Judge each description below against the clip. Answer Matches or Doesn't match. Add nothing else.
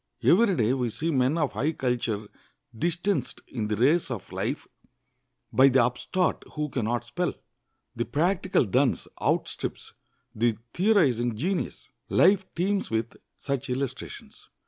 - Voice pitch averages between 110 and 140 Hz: Matches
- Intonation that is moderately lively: Doesn't match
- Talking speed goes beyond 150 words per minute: Doesn't match